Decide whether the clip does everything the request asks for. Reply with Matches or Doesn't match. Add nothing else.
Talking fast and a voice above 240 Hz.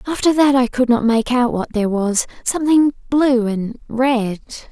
Doesn't match